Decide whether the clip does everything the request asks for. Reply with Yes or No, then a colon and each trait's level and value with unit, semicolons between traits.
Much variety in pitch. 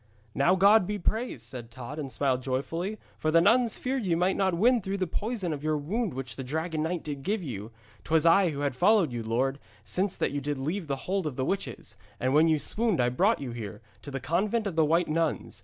Yes: wide, 6.3 semitones